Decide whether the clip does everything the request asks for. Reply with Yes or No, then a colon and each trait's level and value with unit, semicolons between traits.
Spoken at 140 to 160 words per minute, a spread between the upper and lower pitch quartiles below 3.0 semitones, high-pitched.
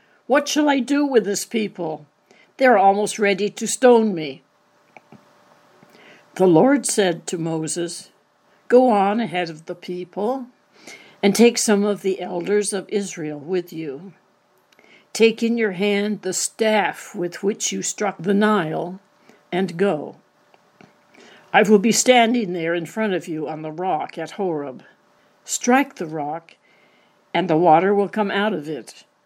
No: average, 150 wpm; average, 3.7 semitones; high, 200 Hz